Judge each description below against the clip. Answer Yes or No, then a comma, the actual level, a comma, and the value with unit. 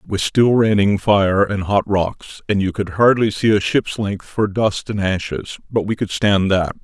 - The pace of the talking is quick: Yes, fast, 220 wpm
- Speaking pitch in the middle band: No, low, 100 Hz